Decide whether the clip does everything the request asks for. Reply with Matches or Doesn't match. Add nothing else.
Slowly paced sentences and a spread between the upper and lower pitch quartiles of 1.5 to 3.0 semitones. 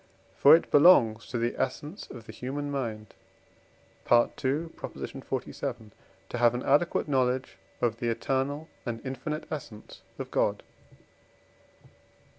Doesn't match